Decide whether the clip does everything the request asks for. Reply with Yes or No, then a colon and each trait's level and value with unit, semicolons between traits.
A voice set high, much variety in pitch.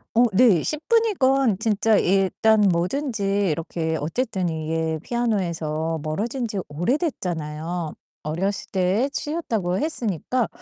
Yes: high, 195 Hz; wide, 6.8 semitones